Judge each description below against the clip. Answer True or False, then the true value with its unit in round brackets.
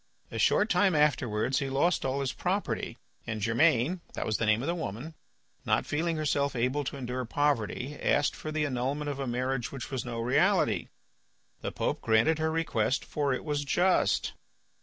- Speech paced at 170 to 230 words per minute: True (180 wpm)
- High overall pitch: False (140 Hz)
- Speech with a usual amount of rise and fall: True (3.9 semitones)